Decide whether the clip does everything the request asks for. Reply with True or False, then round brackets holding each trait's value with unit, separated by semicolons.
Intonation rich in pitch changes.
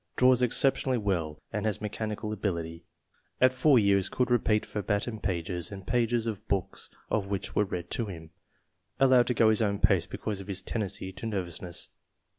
False (3.7 semitones)